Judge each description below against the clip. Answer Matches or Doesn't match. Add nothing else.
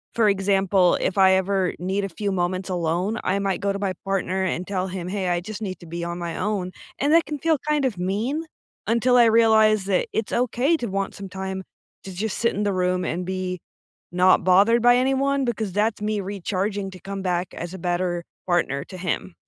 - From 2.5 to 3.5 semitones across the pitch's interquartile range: Matches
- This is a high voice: Matches